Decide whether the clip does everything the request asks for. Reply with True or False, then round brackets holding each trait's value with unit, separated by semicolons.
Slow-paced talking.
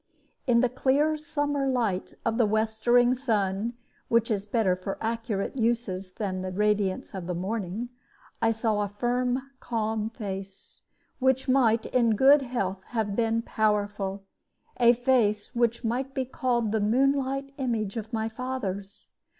False (145 wpm)